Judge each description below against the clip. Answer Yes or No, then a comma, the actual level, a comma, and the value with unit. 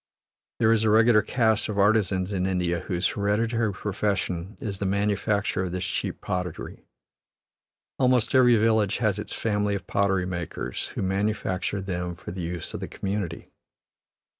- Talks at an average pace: Yes, average, 155 wpm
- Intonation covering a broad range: No, average, 2.8 semitones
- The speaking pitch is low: Yes, low, 100 Hz